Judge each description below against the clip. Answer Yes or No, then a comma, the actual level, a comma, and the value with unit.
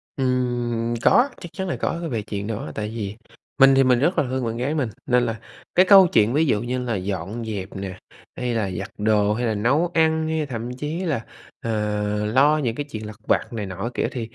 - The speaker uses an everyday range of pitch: Yes, average, 4.4 semitones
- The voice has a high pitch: No, low, 120 Hz